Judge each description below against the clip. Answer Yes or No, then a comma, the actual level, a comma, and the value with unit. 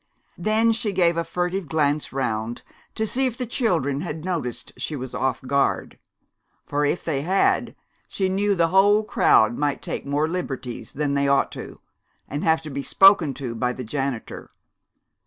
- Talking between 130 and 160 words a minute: No, average, 175 wpm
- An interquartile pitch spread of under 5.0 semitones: No, wide, 5.6 semitones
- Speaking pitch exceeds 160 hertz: No, medium, 150 Hz